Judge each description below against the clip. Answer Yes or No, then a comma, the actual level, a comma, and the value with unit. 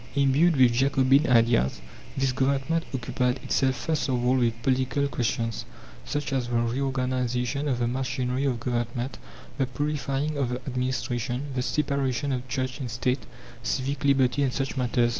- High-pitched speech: No, low, 130 Hz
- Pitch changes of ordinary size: No, narrow, 2.0 semitones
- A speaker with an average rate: Yes, average, 155 wpm